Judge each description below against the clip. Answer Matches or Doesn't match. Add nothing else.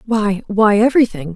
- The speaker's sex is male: Doesn't match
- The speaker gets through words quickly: Doesn't match